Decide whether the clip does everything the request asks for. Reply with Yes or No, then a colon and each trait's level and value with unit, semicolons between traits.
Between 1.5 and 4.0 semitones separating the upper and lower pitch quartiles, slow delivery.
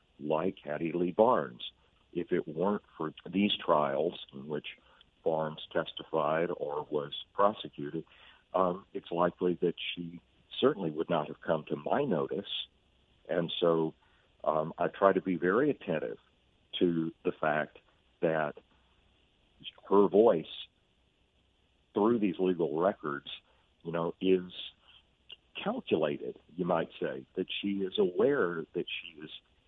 Yes: narrow, 2.6 semitones; slow, 125 wpm